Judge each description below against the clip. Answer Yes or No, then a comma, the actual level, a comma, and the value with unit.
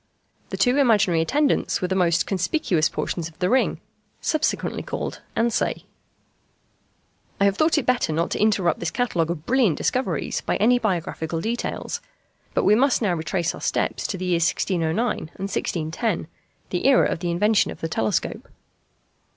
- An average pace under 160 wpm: No, average, 165 wpm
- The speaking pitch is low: No, high, 190 Hz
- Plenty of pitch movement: Yes, wide, 5.9 semitones